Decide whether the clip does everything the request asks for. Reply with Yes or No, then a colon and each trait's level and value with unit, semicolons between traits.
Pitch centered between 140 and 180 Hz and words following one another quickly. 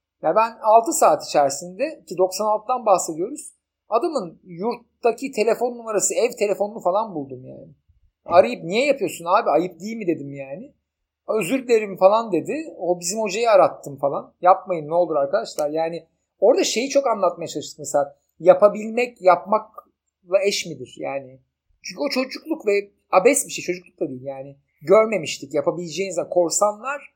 No: high, 190 Hz; fast, 145 wpm